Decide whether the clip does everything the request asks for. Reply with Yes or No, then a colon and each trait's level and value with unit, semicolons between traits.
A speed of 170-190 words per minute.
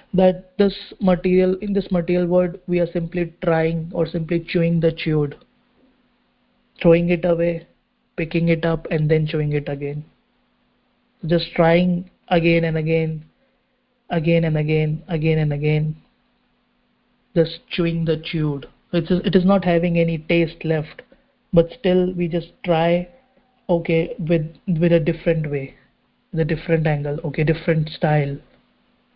No: average, 140 wpm